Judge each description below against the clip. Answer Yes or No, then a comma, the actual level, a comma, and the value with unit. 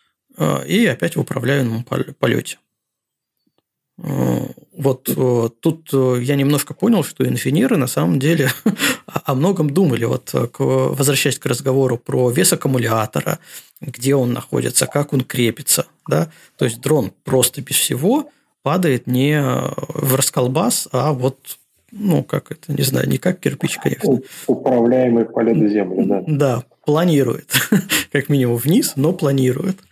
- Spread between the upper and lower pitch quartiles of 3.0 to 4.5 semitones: Yes, average, 3.4 semitones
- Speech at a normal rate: Yes, average, 130 wpm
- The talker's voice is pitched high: No, medium, 140 Hz